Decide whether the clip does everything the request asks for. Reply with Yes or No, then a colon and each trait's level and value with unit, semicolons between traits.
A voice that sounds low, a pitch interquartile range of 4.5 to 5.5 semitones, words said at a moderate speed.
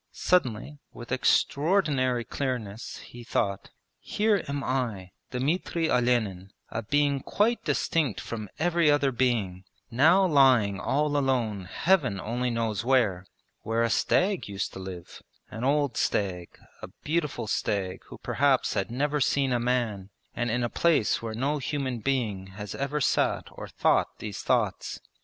Yes: low, 125 Hz; average, 5.2 semitones; average, 145 wpm